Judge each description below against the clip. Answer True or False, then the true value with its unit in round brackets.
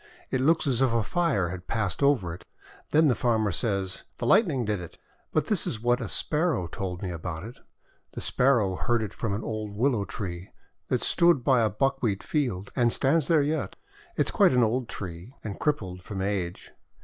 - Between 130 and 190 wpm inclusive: False (205 wpm)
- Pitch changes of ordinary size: False (5.8 semitones)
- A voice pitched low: True (115 Hz)